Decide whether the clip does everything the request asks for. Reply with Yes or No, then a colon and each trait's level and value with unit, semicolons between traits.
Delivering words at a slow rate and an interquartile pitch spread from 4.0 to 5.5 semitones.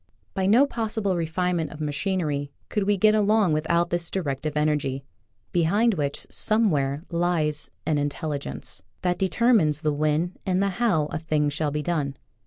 No: average, 170 wpm; average, 4.4 semitones